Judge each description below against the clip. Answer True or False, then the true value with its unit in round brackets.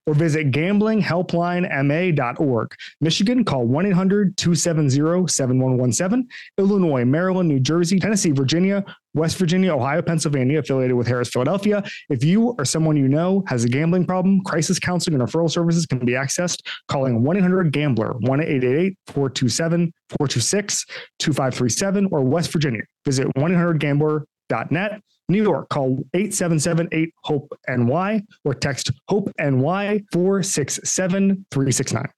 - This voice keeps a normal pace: False (125 wpm)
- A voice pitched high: False (160 Hz)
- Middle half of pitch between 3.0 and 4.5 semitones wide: False (5.1 semitones)